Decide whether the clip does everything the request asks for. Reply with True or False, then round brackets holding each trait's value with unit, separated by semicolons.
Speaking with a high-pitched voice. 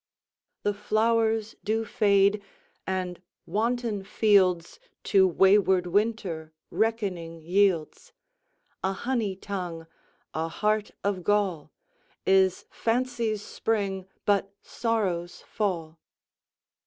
True (200 Hz)